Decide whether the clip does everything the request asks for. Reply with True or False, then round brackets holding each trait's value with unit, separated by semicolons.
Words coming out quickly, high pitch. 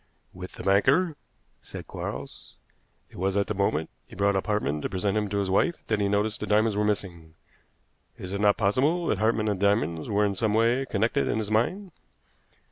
False (210 wpm; 105 Hz)